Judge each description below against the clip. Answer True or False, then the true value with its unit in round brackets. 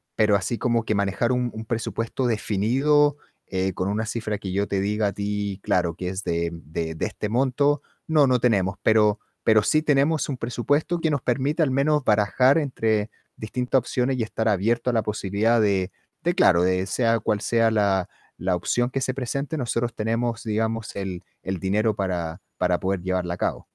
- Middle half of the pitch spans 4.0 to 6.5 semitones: True (4.3 semitones)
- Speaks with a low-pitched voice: True (110 Hz)